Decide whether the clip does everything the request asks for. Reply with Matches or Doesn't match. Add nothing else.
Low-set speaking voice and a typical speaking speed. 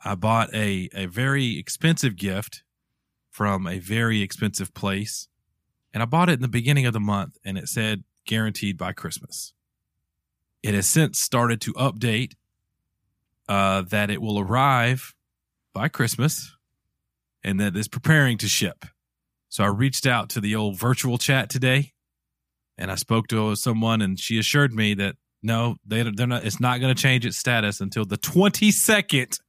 Matches